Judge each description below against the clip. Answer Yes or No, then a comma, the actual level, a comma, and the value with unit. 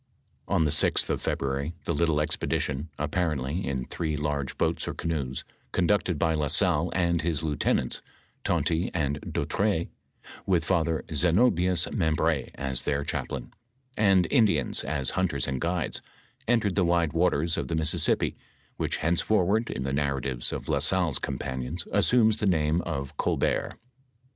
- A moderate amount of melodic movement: Yes, average, 3.9 semitones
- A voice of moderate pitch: No, very low, 80 Hz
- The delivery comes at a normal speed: Yes, average, 145 wpm